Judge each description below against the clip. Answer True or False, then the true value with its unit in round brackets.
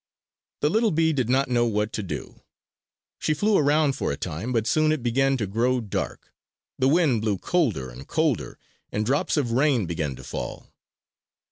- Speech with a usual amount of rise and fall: False (5.9 semitones)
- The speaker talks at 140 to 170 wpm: False (180 wpm)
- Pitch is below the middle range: True (125 Hz)